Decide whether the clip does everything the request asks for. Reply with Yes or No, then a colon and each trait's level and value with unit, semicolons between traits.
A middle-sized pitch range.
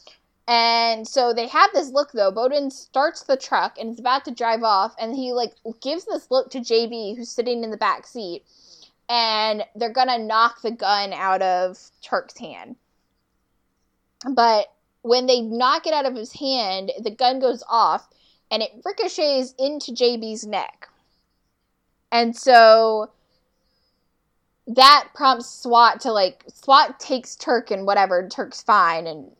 Yes: average, 3.1 semitones